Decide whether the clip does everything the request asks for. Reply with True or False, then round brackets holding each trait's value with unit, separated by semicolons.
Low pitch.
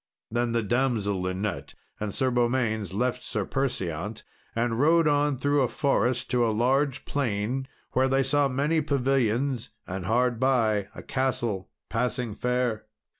True (125 Hz)